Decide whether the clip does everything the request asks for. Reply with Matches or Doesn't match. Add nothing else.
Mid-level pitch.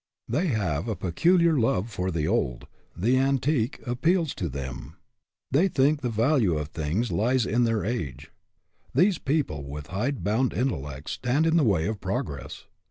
Doesn't match